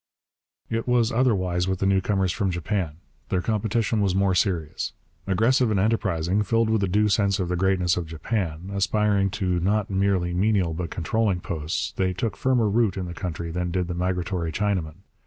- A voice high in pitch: No, very low, 95 Hz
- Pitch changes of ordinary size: Yes, average, 3.1 semitones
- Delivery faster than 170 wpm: Yes, average, 180 wpm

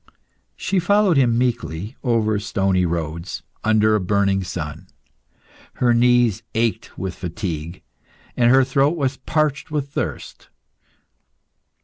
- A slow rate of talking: Yes, slow, 115 wpm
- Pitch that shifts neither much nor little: No, wide, 6.0 semitones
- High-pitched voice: No, low, 115 Hz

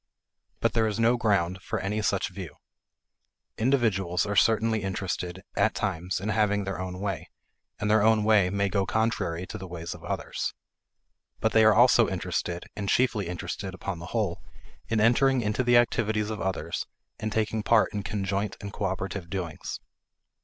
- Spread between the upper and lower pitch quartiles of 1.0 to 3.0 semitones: Yes, average, 2.7 semitones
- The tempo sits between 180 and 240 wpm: No, average, 170 wpm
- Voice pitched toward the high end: No, low, 100 Hz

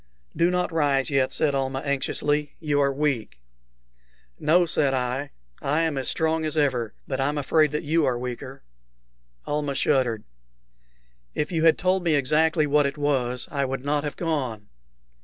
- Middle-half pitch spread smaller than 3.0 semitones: Yes, narrow, 2.6 semitones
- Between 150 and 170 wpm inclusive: Yes, average, 165 wpm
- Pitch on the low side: No, medium, 145 Hz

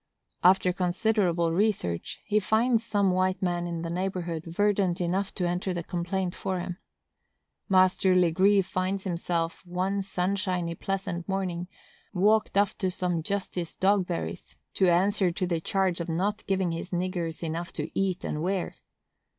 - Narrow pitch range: Yes, narrow, 2.0 semitones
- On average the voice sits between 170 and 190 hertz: Yes, medium, 185 Hz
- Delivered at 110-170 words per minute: Yes, average, 150 wpm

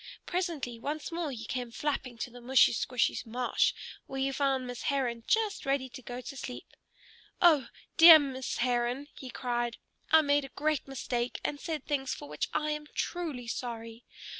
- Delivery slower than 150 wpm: No, average, 175 wpm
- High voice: Yes, very high, 265 Hz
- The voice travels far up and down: No, average, 3.4 semitones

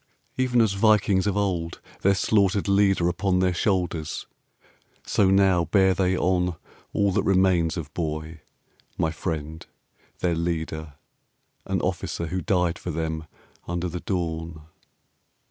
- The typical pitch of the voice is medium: No, very low, 90 Hz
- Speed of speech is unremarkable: No, slow, 130 wpm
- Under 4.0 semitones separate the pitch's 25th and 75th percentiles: Yes, average, 2.9 semitones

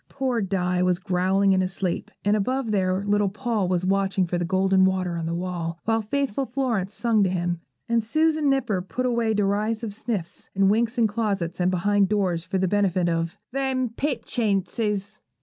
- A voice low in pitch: No, high, 200 Hz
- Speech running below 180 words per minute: No, average, 185 wpm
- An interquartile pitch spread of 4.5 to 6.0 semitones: No, average, 3.7 semitones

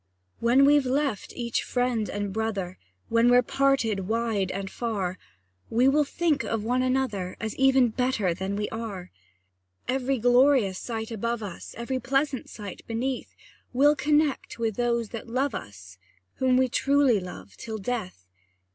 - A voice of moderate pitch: No, high, 235 Hz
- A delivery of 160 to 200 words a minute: No, average, 150 wpm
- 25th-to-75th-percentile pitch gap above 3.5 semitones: Yes, average, 4.2 semitones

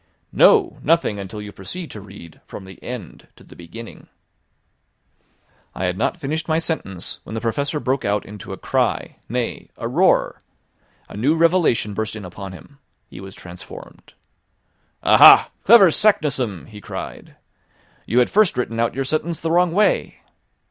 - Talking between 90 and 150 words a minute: No, average, 160 wpm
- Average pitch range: No, wide, 8.3 semitones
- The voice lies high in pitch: No, low, 120 Hz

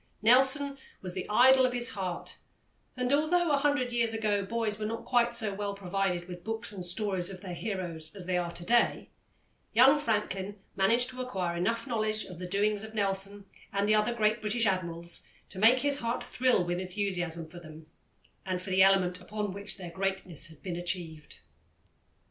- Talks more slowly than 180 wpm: No, average, 190 wpm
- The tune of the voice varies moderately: Yes, average, 4.3 semitones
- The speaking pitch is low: No, high, 200 Hz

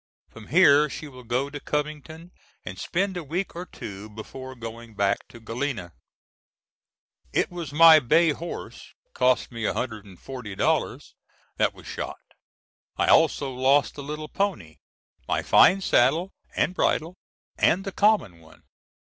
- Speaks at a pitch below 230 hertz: Yes, medium, 140 Hz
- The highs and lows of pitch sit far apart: Yes, wide, 6.2 semitones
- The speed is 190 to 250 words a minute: No, average, 140 wpm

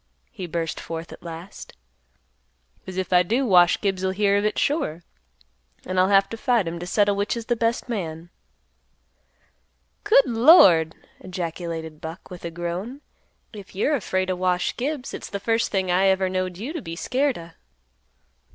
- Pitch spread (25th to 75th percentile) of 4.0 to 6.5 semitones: Yes, average, 4.6 semitones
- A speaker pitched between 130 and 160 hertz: No, medium, 185 Hz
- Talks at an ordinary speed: Yes, average, 170 wpm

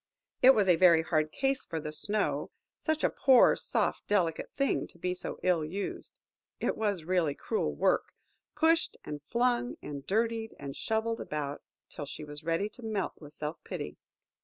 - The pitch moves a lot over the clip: Yes, wide, 6.9 semitones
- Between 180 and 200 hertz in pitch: Yes, medium, 185 Hz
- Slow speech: No, average, 170 wpm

